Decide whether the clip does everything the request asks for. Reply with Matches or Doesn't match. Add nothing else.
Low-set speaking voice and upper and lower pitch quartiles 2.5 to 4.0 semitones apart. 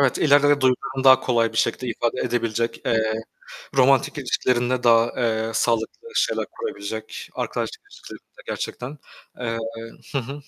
Matches